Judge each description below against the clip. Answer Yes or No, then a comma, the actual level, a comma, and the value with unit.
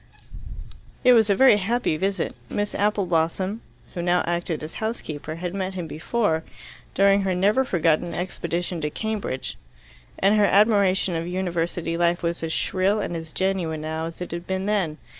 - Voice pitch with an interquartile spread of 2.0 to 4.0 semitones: Yes, average, 3.3 semitones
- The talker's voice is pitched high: No, medium, 180 Hz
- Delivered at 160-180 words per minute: Yes, average, 165 wpm